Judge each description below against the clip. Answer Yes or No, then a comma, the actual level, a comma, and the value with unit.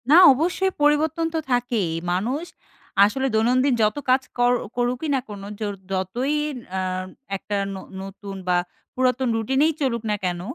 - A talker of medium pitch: No, high, 245 Hz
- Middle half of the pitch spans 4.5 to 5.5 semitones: Yes, average, 4.8 semitones